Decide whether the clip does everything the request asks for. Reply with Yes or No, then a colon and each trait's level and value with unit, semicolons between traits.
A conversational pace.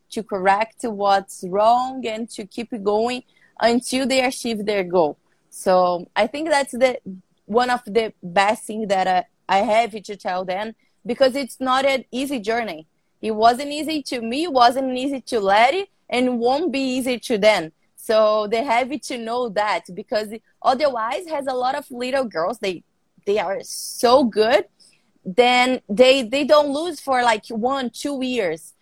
Yes: average, 170 wpm